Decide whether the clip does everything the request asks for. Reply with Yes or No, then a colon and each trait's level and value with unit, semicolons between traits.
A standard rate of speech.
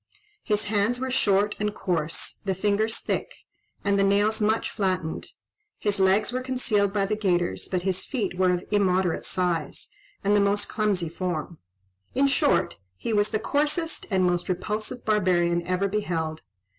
Yes: average, 160 wpm